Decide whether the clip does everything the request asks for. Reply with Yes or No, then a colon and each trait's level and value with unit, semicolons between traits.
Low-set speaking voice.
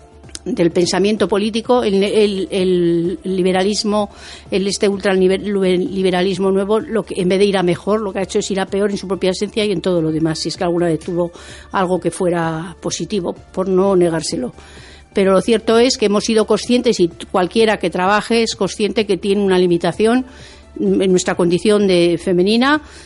No: high, 195 Hz